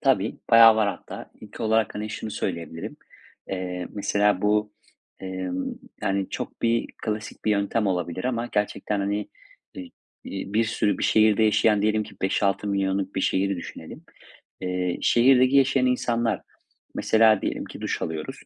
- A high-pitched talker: No, low, 105 Hz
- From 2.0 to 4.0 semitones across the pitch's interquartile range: Yes, average, 2.7 semitones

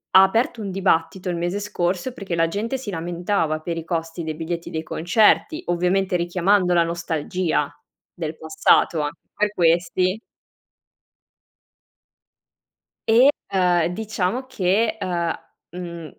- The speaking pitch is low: No, medium, 180 Hz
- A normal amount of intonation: Yes, average, 3.1 semitones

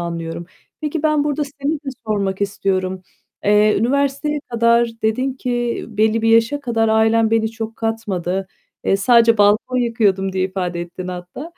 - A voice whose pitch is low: No, high, 225 Hz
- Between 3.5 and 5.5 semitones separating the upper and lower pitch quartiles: Yes, average, 4.1 semitones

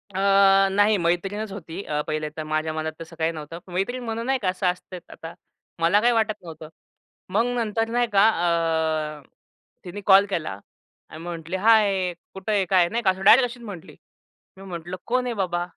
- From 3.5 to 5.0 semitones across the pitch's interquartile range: Yes, average, 4.4 semitones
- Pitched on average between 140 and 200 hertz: Yes, medium, 185 Hz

